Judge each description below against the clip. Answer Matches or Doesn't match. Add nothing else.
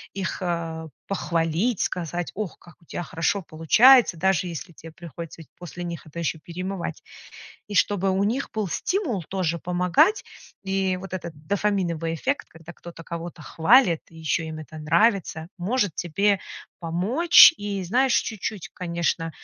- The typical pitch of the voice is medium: Matches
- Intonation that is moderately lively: Matches